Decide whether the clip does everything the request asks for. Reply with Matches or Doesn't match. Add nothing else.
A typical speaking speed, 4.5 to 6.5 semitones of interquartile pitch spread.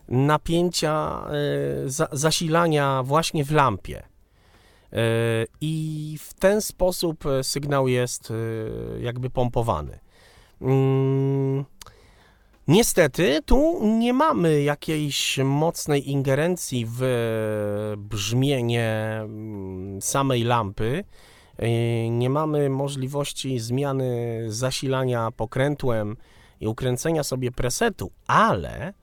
Doesn't match